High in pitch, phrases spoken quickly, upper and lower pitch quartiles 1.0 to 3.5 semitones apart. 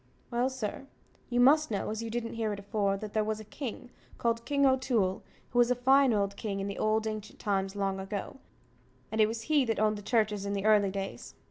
Yes: high, 215 Hz; fast, 230 wpm; average, 3.1 semitones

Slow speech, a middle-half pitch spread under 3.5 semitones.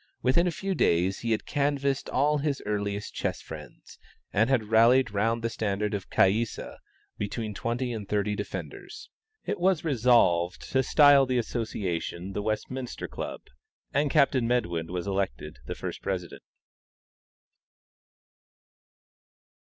No: slow, 130 wpm; average, 4.8 semitones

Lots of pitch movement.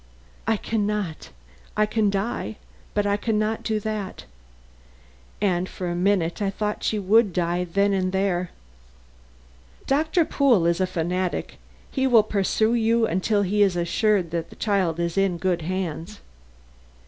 No: average, 3.2 semitones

